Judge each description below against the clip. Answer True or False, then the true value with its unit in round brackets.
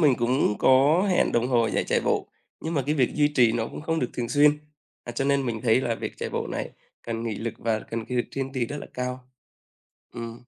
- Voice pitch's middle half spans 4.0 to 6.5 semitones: False (3.2 semitones)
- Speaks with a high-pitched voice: False (125 Hz)